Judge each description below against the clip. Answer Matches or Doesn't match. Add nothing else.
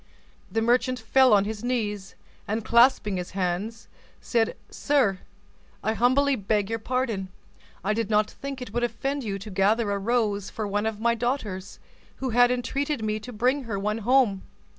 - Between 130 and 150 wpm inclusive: Doesn't match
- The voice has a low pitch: Doesn't match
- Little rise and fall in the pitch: Doesn't match